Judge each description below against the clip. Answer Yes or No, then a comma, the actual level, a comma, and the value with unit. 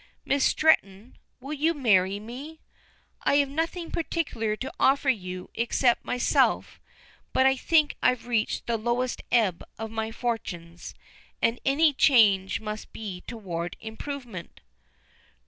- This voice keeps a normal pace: No, slow, 130 wpm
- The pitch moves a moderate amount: Yes, average, 4.6 semitones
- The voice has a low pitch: No, high, 235 Hz